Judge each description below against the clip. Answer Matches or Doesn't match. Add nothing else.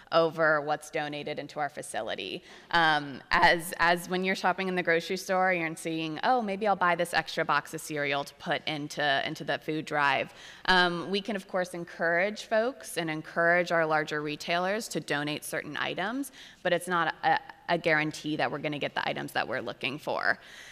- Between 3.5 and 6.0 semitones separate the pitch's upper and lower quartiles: Doesn't match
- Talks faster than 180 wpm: Matches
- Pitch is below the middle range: Doesn't match